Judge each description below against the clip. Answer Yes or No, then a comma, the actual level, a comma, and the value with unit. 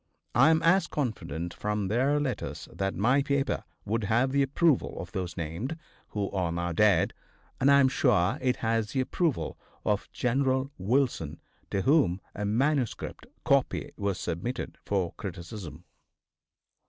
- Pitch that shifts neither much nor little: No, wide, 6.3 semitones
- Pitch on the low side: Yes, low, 115 Hz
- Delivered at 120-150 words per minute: Yes, average, 145 wpm